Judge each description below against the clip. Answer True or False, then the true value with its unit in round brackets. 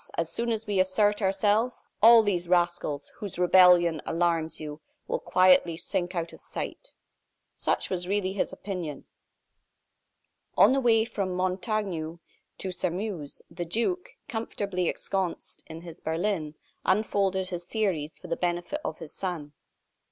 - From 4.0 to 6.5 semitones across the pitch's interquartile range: False (3.4 semitones)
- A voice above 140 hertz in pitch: True (185 Hz)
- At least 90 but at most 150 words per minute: True (140 wpm)